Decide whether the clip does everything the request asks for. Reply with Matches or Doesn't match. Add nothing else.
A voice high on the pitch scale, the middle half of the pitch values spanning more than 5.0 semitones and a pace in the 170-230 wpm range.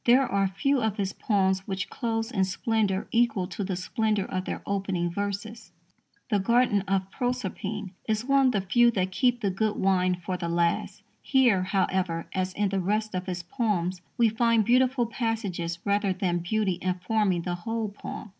Doesn't match